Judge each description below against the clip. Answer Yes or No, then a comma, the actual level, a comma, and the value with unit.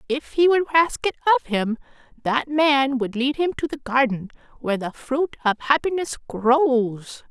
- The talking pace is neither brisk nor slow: Yes, average, 170 wpm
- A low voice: No, very high, 270 Hz